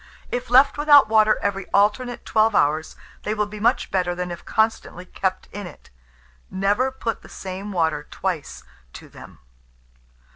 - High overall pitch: Yes, high, 205 Hz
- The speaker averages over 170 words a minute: No, average, 155 wpm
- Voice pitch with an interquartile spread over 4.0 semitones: No, average, 3.5 semitones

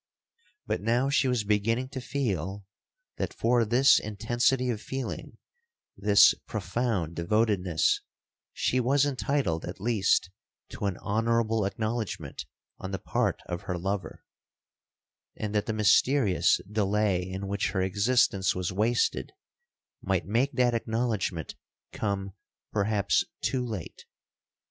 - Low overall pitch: Yes, low, 105 Hz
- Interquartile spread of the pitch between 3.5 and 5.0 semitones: Yes, average, 3.8 semitones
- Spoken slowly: Yes, slow, 120 wpm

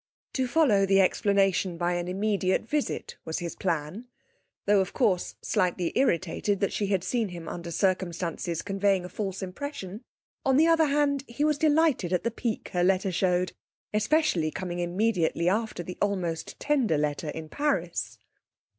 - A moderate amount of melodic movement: Yes, average, 4.9 semitones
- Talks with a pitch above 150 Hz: Yes, high, 190 Hz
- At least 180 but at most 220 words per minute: No, average, 160 wpm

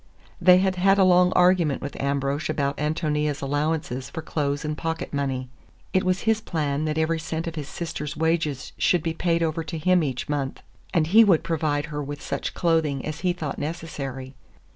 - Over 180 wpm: Yes, average, 190 wpm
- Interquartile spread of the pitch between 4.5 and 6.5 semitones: No, average, 2.8 semitones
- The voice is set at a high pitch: No, medium, 155 Hz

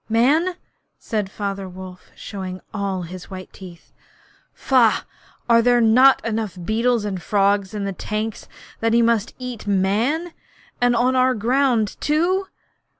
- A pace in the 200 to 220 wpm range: No, average, 140 wpm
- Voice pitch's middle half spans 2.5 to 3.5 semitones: No, average, 4.1 semitones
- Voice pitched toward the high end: Yes, high, 220 Hz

